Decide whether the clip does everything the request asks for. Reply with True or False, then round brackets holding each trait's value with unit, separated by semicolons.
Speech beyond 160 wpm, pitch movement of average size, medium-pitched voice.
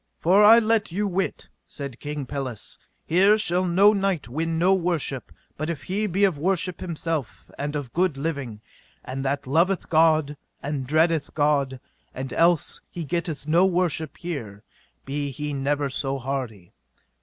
False (155 wpm; 4.4 semitones; 155 Hz)